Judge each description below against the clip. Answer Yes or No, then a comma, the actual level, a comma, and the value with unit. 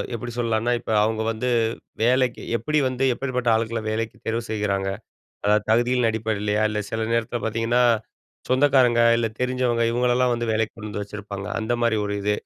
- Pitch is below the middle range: Yes, low, 115 Hz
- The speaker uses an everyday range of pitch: No, narrow, 2.2 semitones